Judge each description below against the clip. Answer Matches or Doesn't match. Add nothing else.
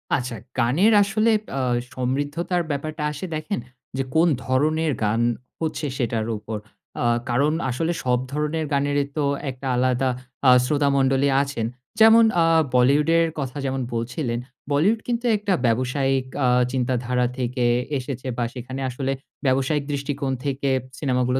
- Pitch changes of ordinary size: Matches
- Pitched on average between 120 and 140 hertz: Matches